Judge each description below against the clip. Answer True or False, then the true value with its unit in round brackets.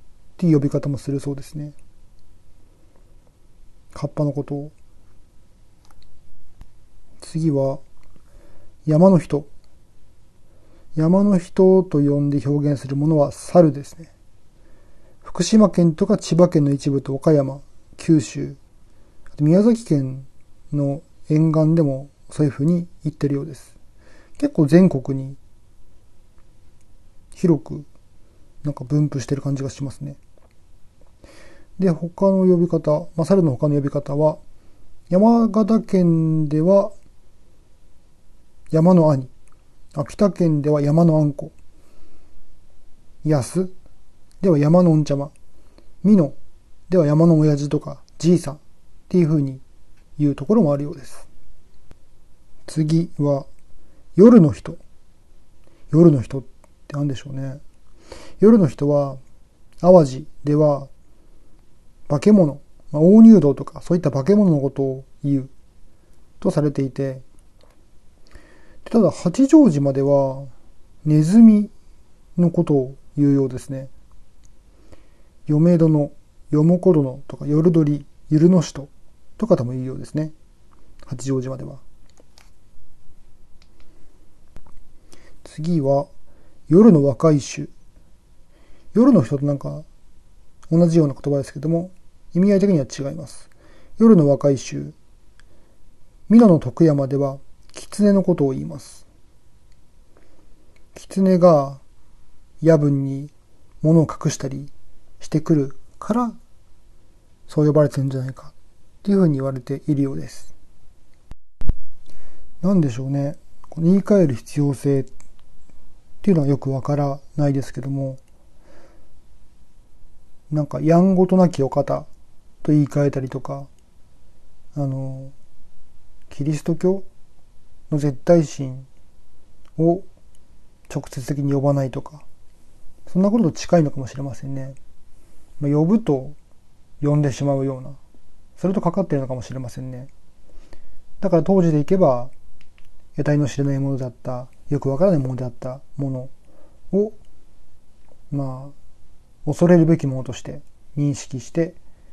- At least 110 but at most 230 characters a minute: True (225 characters per minute)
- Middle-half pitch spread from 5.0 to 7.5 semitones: True (6.5 semitones)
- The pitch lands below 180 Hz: True (140 Hz)